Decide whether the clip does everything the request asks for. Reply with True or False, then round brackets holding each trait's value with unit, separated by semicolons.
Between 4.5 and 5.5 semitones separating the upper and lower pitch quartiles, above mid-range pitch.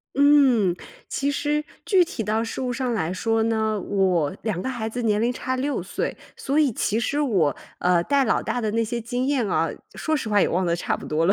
True (5.1 semitones; 225 Hz)